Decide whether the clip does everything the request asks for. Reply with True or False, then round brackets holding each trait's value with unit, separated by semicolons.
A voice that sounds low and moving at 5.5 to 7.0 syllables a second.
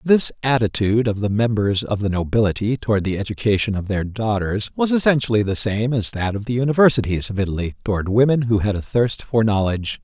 True (110 Hz; 6.0 syllables/s)